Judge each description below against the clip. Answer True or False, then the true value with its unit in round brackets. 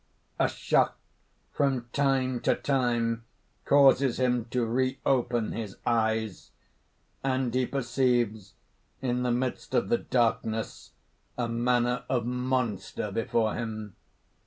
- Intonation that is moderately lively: False (2.1 semitones)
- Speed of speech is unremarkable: False (110 wpm)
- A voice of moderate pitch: False (120 Hz)